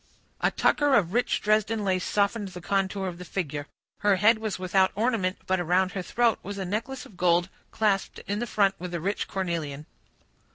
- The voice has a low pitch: No, high, 195 Hz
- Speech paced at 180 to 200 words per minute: Yes, average, 190 wpm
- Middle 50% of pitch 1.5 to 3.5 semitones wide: Yes, average, 2.9 semitones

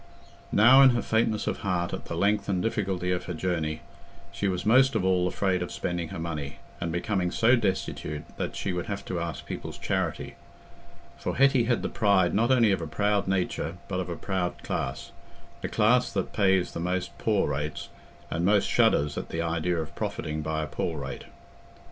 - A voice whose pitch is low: Yes, very low, 90 Hz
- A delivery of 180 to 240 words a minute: Yes, average, 195 wpm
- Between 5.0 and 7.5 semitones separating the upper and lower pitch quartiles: No, average, 3.7 semitones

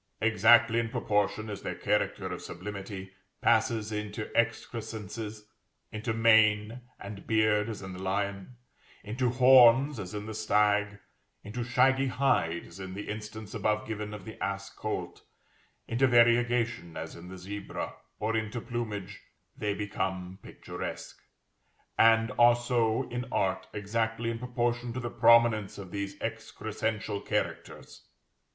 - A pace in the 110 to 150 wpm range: Yes, slow, 135 wpm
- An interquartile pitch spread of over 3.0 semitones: No, narrow, 2.4 semitones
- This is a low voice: Yes, low, 110 Hz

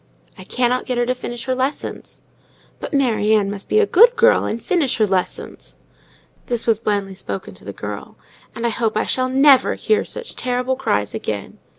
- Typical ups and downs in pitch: Yes, average, 3.8 semitones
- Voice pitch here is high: Yes, high, 245 Hz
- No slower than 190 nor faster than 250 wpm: Yes, average, 195 wpm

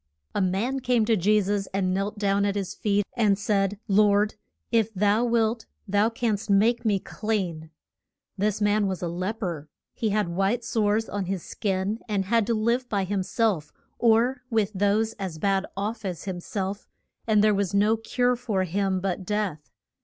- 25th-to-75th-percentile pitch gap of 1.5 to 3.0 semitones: Yes, narrow, 2.4 semitones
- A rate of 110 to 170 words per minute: No, average, 185 wpm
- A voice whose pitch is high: Yes, high, 205 Hz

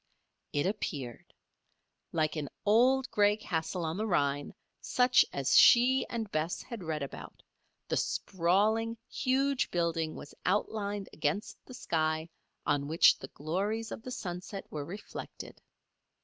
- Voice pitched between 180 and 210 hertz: Yes, medium, 185 Hz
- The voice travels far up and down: Yes, wide, 5.9 semitones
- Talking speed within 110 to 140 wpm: Yes, slow, 135 wpm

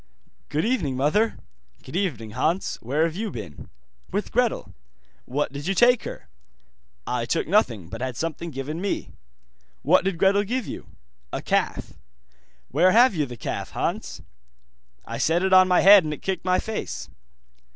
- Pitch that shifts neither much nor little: No, wide, 6.2 semitones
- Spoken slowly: No, average, 165 wpm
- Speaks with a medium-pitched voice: Yes, medium, 165 Hz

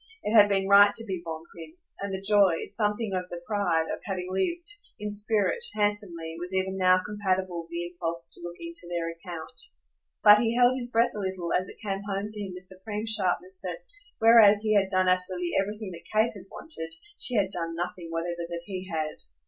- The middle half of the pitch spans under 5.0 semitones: Yes, average, 3.3 semitones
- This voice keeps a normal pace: No, fast, 210 wpm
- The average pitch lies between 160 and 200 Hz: Yes, high, 190 Hz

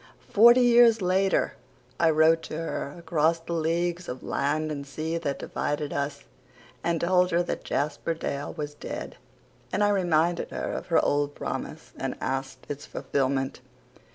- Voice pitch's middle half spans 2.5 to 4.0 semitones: Yes, average, 3.3 semitones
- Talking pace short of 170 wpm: Yes, average, 155 wpm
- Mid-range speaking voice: Yes, medium, 160 Hz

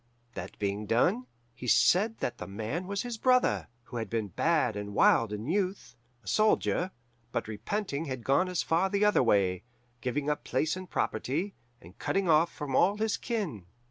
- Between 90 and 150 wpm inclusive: No, average, 180 wpm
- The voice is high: No, medium, 145 Hz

